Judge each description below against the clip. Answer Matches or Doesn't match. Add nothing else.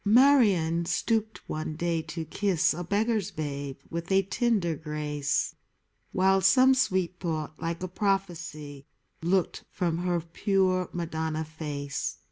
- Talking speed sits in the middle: Doesn't match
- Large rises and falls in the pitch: Doesn't match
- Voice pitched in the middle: Matches